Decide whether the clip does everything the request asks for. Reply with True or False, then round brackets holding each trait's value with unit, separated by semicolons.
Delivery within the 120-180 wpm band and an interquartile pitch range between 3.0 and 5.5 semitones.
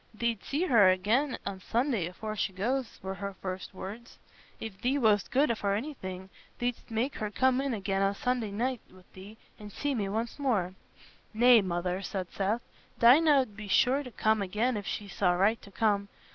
False (190 wpm; 4.2 semitones)